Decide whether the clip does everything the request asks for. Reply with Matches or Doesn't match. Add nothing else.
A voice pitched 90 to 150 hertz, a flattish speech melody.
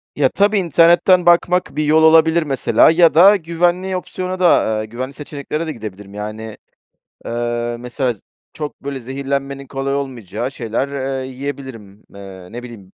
Doesn't match